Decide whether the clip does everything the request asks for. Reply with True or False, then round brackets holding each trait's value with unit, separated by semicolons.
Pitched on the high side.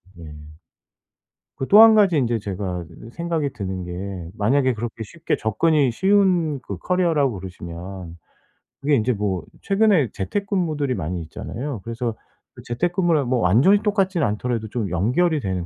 False (125 Hz)